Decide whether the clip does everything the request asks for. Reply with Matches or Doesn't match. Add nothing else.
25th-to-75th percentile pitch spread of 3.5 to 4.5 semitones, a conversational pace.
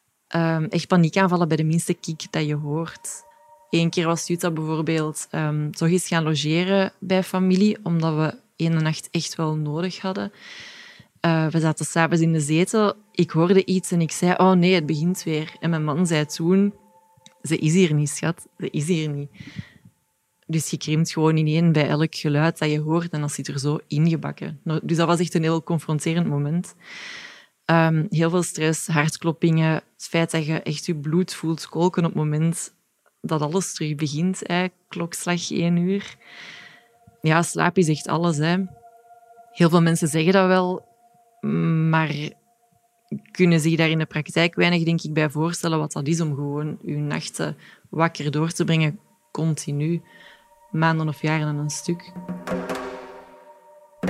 Doesn't match